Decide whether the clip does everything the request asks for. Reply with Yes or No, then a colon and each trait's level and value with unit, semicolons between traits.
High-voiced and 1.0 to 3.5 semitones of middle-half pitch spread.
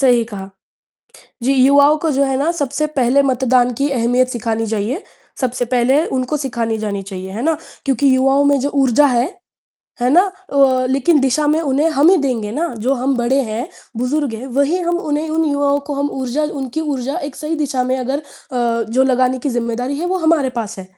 Yes: very high, 265 Hz; average, 2.9 semitones